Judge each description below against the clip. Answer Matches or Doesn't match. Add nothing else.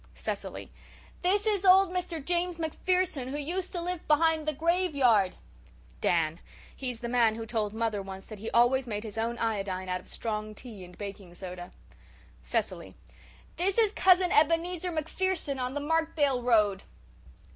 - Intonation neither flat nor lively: Doesn't match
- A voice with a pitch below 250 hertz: Doesn't match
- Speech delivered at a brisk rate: Doesn't match